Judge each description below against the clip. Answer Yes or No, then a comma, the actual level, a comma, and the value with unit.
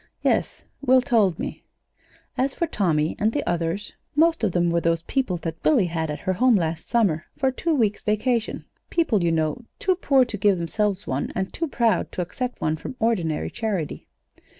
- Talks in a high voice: Yes, high, 205 Hz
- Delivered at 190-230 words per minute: Yes, average, 195 wpm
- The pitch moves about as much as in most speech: No, wide, 7.1 semitones